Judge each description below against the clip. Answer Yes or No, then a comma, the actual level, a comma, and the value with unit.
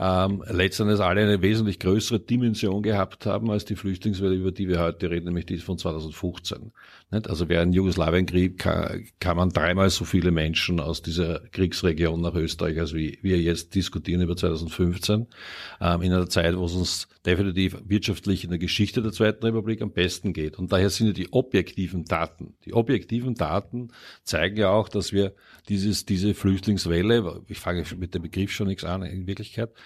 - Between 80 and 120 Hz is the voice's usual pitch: Yes, very low, 95 Hz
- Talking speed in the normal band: Yes, average, 175 wpm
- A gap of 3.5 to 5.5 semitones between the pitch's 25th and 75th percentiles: No, average, 3.0 semitones